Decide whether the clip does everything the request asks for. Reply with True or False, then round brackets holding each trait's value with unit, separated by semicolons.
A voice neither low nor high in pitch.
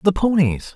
True (170 Hz)